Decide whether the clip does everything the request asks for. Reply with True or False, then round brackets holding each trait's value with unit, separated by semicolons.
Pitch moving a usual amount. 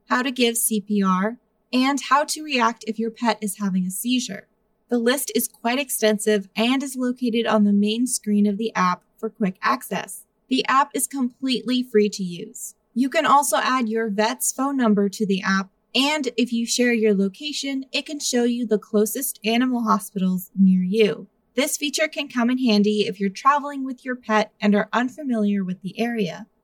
True (3.0 semitones)